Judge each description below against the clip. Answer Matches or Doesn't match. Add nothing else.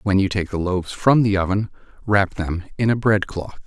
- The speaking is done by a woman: Doesn't match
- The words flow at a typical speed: Doesn't match